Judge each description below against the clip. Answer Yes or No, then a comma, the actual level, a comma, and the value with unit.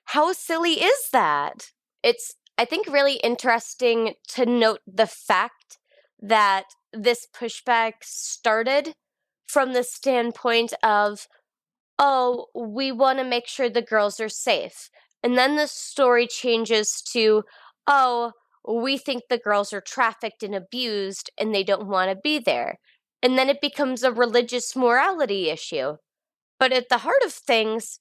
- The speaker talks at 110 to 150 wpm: Yes, average, 145 wpm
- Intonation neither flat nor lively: Yes, average, 3.7 semitones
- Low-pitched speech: No, high, 245 Hz